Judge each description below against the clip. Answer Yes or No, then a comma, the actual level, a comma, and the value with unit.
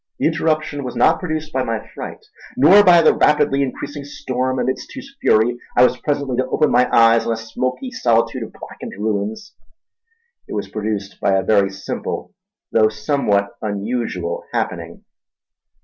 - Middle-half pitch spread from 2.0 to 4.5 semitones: No, average, 5.3 semitones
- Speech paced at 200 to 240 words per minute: No, average, 160 wpm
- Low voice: Yes, low, 125 Hz